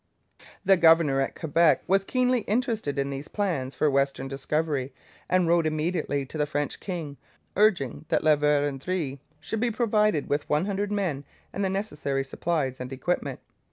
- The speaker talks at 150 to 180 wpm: Yes, average, 160 wpm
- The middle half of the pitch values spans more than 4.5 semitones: Yes, wide, 5.4 semitones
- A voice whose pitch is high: No, medium, 155 Hz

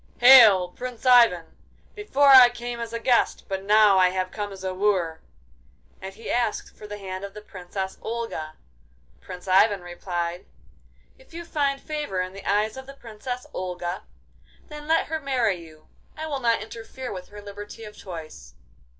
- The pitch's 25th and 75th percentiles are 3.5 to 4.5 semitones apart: No, average, 5.0 semitones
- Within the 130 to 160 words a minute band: No, average, 175 wpm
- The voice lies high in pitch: Yes, high, 210 Hz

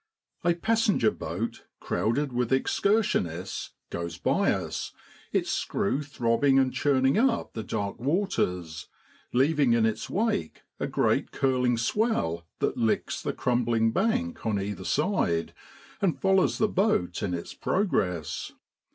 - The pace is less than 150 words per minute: Yes, slow, 135 wpm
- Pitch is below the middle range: Yes, low, 125 Hz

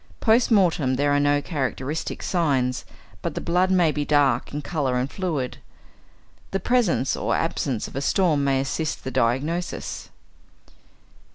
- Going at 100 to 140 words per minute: No, average, 150 wpm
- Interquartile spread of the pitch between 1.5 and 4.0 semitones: No, average, 4.7 semitones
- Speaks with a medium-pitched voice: Yes, medium, 145 Hz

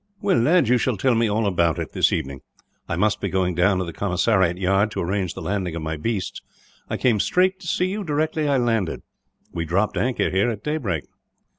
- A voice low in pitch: Yes, low, 105 Hz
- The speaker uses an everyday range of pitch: No, wide, 6.2 semitones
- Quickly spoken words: Yes, fast, 220 wpm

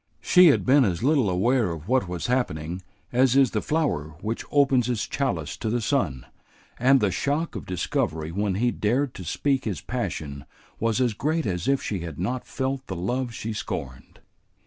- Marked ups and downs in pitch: Yes, wide, 6.9 semitones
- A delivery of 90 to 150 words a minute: No, average, 190 wpm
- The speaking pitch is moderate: No, low, 115 Hz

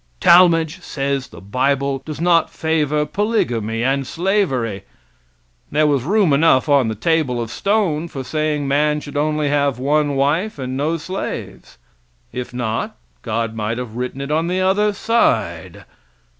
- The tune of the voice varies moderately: Yes, average, 4.4 semitones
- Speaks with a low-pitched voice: No, medium, 145 Hz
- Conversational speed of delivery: Yes, average, 150 wpm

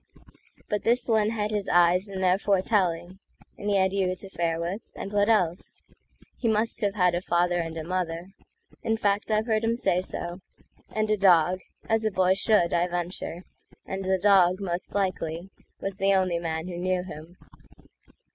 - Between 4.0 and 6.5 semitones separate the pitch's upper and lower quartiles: No, average, 2.9 semitones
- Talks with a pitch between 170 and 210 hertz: Yes, medium, 185 Hz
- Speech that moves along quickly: No, average, 165 wpm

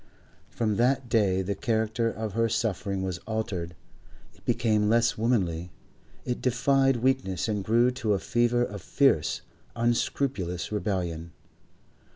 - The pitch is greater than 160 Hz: No, low, 110 Hz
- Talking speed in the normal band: No, slow, 130 wpm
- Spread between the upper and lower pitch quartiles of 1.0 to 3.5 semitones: No, average, 4.0 semitones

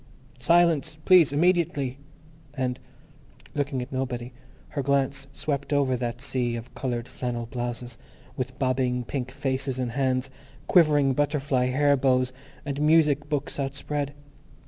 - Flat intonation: Yes, narrow, 2.3 semitones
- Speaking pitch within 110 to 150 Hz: Yes, low, 135 Hz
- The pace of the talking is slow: Yes, slow, 125 wpm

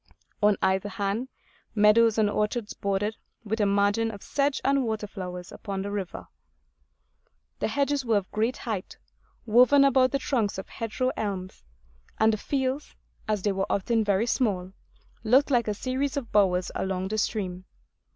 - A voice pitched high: Yes, high, 215 Hz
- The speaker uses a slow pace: No, average, 160 wpm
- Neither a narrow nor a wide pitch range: Yes, average, 3.5 semitones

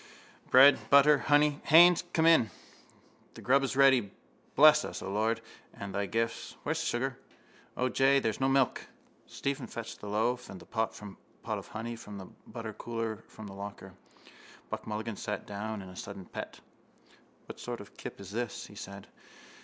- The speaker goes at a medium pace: Yes, average, 175 wpm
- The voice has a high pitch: No, low, 115 Hz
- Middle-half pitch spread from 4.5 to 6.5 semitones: Yes, average, 5.0 semitones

